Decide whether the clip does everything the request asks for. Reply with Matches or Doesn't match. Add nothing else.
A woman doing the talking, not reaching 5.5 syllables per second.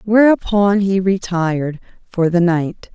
Matches